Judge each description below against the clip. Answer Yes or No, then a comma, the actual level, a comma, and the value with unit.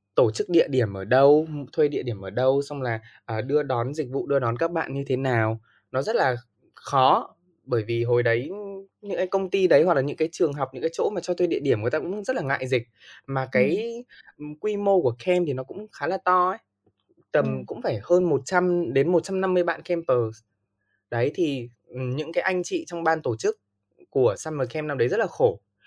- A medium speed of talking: Yes, average, 225 wpm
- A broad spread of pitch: Yes, wide, 6.1 semitones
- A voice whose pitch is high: No, medium, 150 Hz